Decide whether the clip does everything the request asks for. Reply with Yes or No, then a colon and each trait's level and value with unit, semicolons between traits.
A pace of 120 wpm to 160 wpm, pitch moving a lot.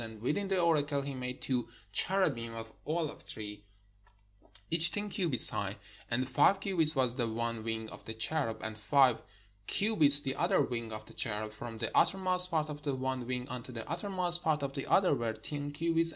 No: average, 195 wpm; wide, 6.1 semitones